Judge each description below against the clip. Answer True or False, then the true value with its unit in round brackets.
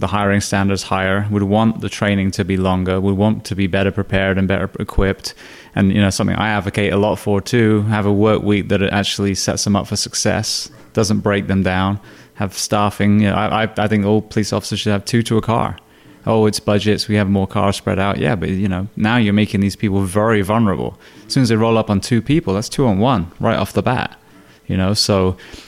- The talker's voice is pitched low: True (105 Hz)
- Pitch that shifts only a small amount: True (1.6 semitones)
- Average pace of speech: False (235 wpm)